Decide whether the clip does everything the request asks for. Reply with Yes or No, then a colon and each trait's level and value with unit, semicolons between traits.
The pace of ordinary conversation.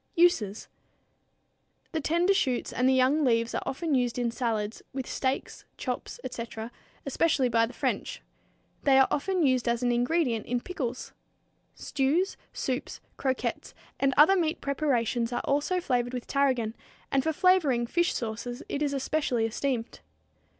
Yes: average, 150 wpm